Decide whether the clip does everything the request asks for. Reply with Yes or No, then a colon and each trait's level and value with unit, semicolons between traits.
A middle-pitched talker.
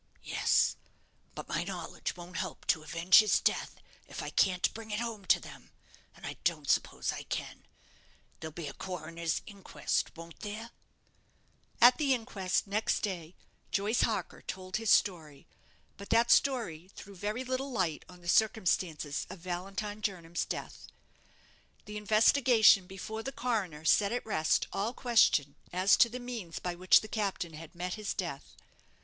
No: high, 195 Hz